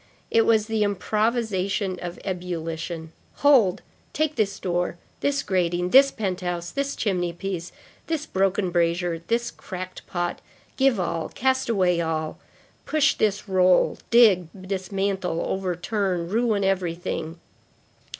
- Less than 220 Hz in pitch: Yes, high, 190 Hz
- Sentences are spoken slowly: Yes, slow, 120 wpm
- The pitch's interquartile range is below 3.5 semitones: No, average, 3.8 semitones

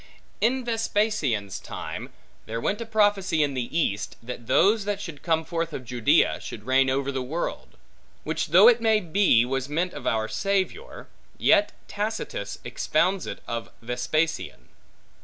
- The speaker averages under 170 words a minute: Yes, average, 155 wpm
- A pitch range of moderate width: No, wide, 8.7 semitones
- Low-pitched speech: No, medium, 160 Hz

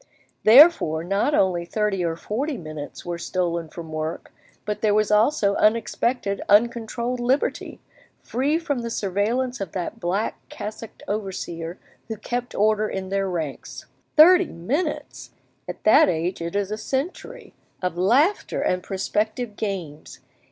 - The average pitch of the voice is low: No, high, 210 Hz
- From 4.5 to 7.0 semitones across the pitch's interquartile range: Yes, average, 5.1 semitones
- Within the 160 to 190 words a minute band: No, slow, 135 wpm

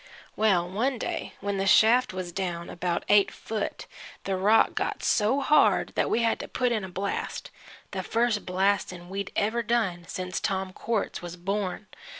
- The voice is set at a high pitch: Yes, high, 200 Hz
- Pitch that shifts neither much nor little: Yes, average, 3.2 semitones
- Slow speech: No, average, 170 wpm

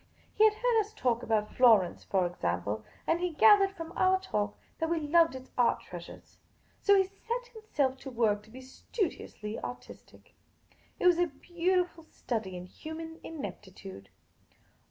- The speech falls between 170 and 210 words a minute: No, average, 155 wpm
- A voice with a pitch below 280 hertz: No, very high, 310 Hz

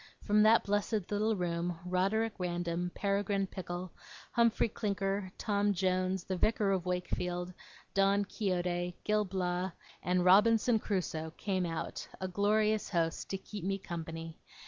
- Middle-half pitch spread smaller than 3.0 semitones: Yes, narrow, 2.5 semitones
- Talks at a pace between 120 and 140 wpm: Yes, slow, 135 wpm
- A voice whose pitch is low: No, high, 190 Hz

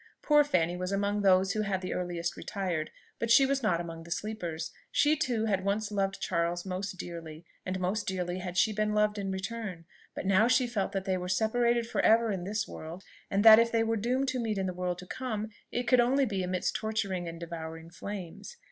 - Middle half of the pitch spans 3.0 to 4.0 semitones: Yes, average, 3.6 semitones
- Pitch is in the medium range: No, high, 195 Hz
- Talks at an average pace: No, fast, 220 wpm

